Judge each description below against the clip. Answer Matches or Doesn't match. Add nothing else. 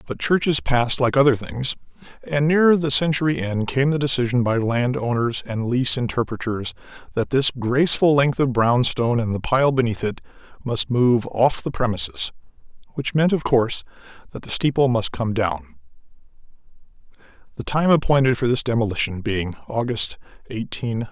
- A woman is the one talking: Doesn't match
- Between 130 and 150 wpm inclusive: Doesn't match